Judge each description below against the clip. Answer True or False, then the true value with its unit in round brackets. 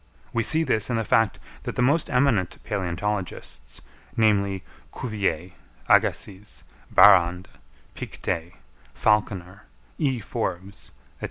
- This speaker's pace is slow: True (105 wpm)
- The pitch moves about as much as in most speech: True (3.6 semitones)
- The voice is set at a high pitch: False (105 Hz)